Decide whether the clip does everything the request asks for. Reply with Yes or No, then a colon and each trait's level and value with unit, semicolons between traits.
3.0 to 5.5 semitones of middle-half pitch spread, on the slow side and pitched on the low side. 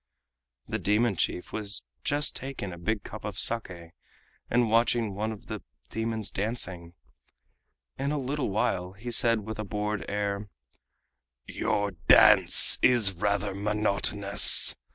No: narrow, 2.5 semitones; slow, 130 wpm; low, 105 Hz